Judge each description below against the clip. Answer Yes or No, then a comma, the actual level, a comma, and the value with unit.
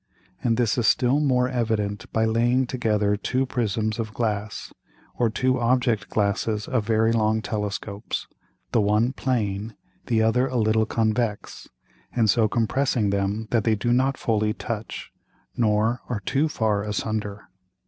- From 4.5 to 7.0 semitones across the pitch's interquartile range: No, narrow, 2.5 semitones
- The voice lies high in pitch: No, low, 110 Hz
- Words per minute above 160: No, average, 150 wpm